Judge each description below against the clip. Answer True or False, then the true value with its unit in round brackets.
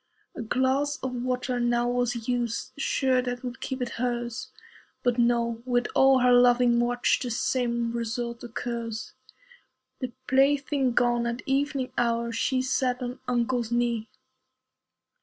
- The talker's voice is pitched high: True (245 Hz)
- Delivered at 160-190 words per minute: False (140 wpm)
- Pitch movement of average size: False (1.3 semitones)